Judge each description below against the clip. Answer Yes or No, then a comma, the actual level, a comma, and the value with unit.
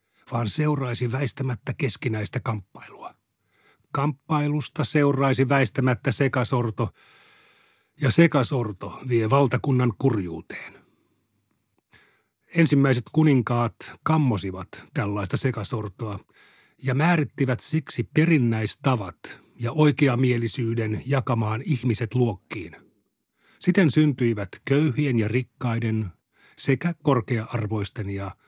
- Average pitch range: Yes, average, 3.6 semitones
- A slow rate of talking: Yes, slow, 75 wpm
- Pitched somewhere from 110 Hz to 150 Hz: Yes, low, 130 Hz